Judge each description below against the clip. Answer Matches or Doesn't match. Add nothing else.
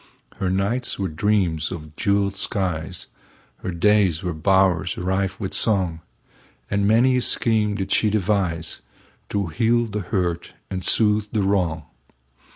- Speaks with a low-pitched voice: Matches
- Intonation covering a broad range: Doesn't match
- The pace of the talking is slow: Matches